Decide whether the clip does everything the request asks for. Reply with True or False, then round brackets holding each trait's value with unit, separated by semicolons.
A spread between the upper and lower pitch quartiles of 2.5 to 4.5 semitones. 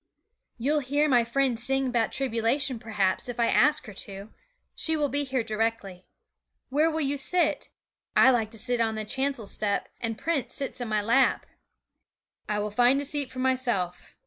True (3.8 semitones)